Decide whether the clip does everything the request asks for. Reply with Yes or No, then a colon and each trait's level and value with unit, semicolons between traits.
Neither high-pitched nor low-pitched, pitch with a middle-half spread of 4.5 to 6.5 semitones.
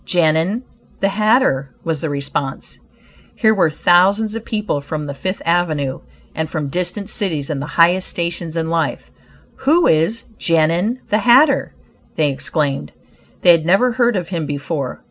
Yes: medium, 170 Hz; wide, 5.4 semitones